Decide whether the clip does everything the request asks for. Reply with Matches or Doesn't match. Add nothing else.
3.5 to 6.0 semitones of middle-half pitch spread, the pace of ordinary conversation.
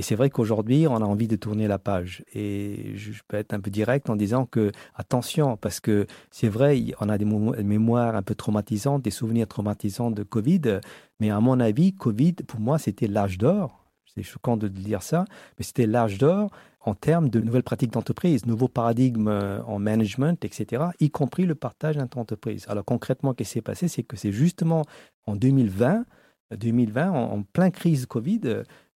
Matches